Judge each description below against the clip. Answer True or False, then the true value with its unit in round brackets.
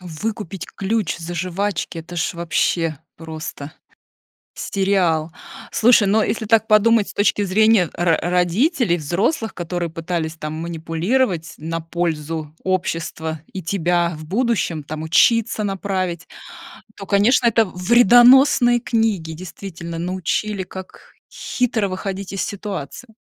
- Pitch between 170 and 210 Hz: True (185 Hz)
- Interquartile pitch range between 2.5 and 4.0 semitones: False (4.4 semitones)